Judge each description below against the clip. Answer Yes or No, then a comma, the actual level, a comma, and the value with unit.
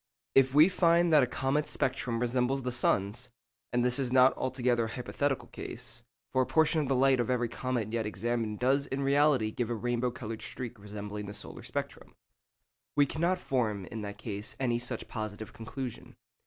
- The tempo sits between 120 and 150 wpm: No, average, 180 wpm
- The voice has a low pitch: Yes, low, 125 Hz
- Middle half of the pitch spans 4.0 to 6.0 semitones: No, average, 3.0 semitones